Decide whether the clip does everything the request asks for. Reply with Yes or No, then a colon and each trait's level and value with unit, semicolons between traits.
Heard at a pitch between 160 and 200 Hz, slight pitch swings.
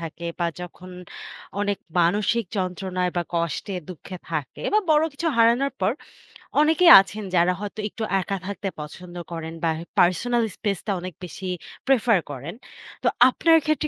No: high, 190 Hz; average, 5.0 semitones